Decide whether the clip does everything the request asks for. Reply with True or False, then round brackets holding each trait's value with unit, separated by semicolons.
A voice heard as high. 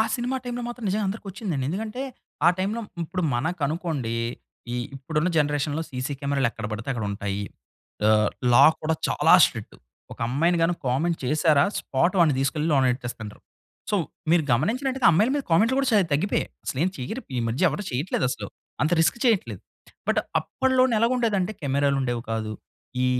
False (160 Hz)